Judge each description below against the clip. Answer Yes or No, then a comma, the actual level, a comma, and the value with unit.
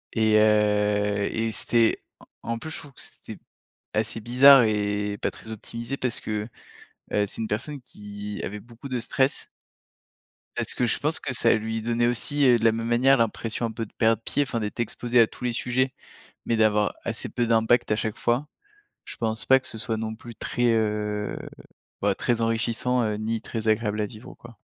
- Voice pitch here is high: No, low, 115 Hz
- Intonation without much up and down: Yes, narrow, 2.1 semitones